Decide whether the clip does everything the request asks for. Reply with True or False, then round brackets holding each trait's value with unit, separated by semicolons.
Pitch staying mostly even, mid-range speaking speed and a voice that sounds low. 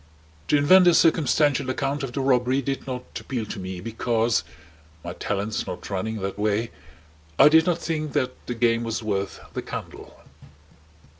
False (4.8 semitones; 165 wpm; 120 Hz)